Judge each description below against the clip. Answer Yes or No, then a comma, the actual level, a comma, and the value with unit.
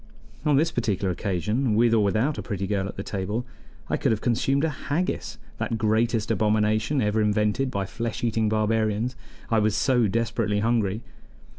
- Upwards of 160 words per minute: Yes, average, 170 wpm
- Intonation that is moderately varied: No, narrow, 2.2 semitones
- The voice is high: No, low, 110 Hz